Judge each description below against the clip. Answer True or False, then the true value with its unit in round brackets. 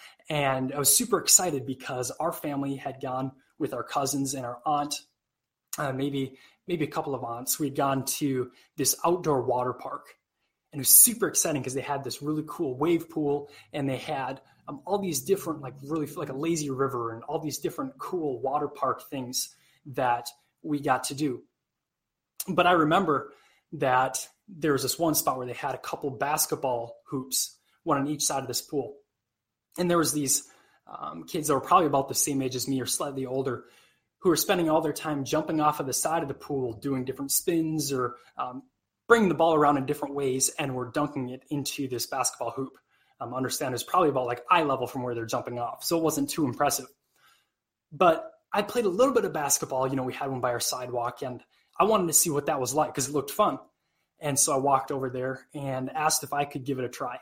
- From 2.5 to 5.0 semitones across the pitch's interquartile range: True (3.1 semitones)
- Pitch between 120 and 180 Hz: True (140 Hz)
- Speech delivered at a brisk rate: True (215 wpm)